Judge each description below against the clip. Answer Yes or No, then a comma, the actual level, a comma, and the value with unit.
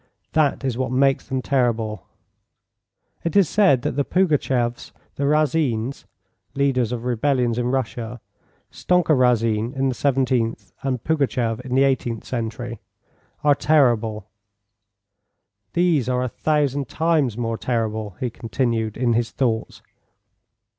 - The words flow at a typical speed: No, slow, 125 wpm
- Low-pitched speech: Yes, low, 125 Hz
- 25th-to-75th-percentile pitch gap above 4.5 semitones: No, average, 3.3 semitones